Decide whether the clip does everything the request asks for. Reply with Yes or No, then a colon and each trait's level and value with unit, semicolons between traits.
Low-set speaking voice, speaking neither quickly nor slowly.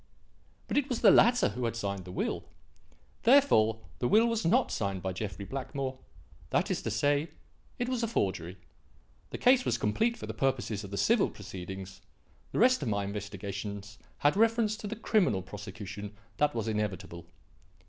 Yes: low, 110 Hz; average, 175 wpm